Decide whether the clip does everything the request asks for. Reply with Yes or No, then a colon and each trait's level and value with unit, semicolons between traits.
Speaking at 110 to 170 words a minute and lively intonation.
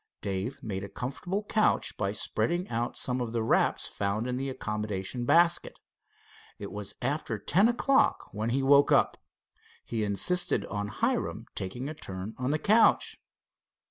Yes: average, 155 wpm; wide, 6.3 semitones